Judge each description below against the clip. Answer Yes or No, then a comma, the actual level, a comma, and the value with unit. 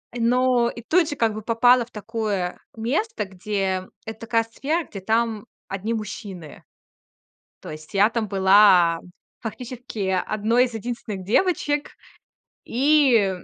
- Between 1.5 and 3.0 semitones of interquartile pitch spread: No, average, 3.6 semitones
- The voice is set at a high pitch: Yes, high, 225 Hz